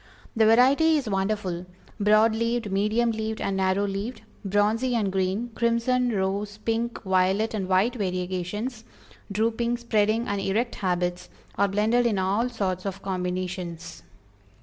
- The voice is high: Yes, high, 210 Hz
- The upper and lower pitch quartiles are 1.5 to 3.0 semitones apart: No, average, 3.4 semitones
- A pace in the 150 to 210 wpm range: No, slow, 135 wpm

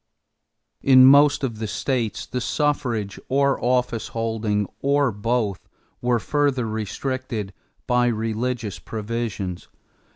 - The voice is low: Yes, low, 120 Hz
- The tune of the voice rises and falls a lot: No, average, 3.1 semitones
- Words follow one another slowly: Yes, slow, 105 wpm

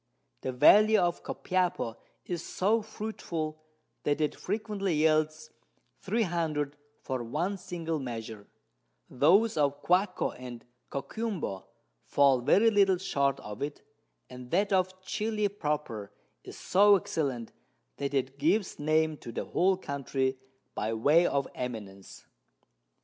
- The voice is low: No, medium, 155 Hz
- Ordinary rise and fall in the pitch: No, wide, 6.2 semitones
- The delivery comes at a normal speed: No, slow, 120 wpm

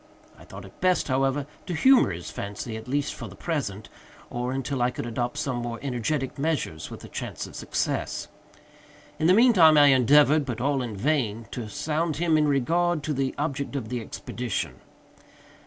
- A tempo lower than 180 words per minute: No, average, 190 wpm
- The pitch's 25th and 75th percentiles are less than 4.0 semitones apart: No, average, 4.3 semitones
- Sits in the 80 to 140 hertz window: Yes, low, 135 Hz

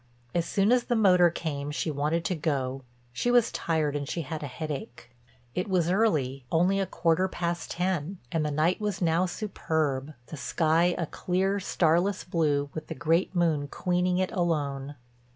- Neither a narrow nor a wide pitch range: Yes, average, 3.9 semitones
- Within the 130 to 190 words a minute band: Yes, average, 170 wpm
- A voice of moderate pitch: Yes, medium, 165 Hz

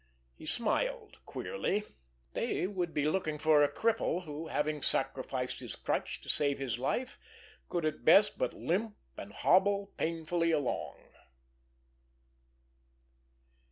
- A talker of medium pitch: Yes, medium, 165 Hz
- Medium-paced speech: No, slow, 125 wpm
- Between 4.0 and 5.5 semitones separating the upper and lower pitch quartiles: Yes, average, 5.1 semitones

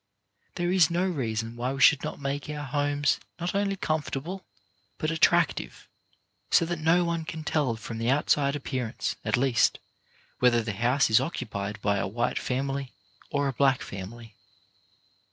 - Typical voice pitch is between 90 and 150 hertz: Yes, medium, 140 Hz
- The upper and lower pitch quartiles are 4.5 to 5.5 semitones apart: Yes, average, 5.1 semitones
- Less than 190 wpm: Yes, average, 160 wpm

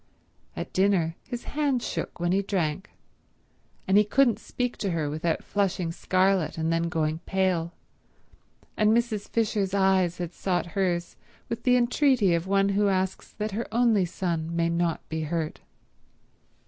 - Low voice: No, high, 190 Hz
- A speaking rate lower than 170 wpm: Yes, average, 155 wpm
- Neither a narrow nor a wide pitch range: Yes, average, 3.8 semitones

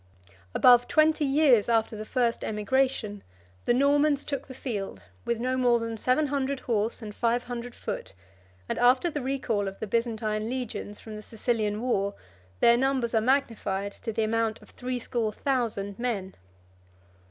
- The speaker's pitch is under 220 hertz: No, high, 235 Hz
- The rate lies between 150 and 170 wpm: Yes, average, 165 wpm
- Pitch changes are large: No, average, 3.3 semitones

